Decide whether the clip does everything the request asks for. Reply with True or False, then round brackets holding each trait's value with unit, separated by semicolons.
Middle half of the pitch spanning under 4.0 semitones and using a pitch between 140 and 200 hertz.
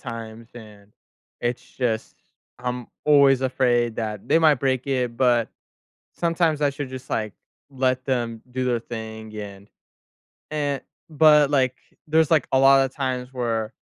False (3.1 semitones; 125 Hz)